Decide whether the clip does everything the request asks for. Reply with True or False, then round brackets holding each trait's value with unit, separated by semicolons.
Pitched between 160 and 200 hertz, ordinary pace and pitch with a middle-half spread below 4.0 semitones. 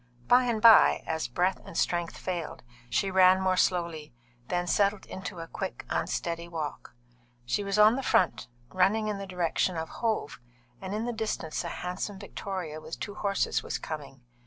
True (185 Hz; 175 wpm; 3.5 semitones)